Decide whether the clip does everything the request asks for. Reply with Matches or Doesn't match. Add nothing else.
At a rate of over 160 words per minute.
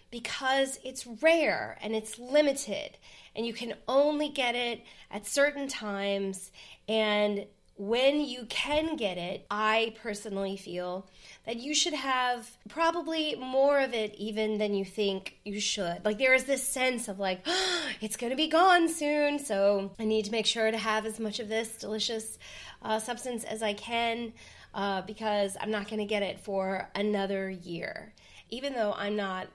Matches